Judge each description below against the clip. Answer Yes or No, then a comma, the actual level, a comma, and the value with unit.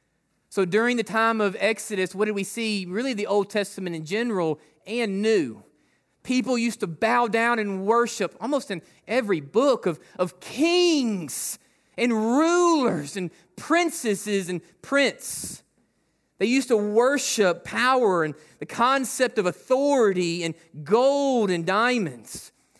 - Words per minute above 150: No, slow, 135 wpm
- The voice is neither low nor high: No, high, 215 Hz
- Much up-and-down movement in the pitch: No, average, 5.0 semitones